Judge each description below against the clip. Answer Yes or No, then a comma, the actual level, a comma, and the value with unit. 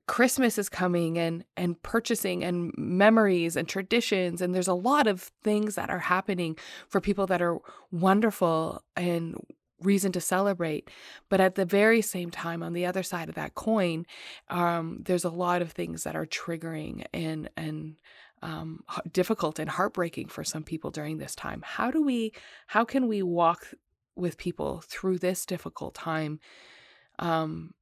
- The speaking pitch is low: No, medium, 180 Hz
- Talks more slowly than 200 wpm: Yes, average, 165 wpm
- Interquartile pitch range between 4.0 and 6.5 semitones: No, average, 3.0 semitones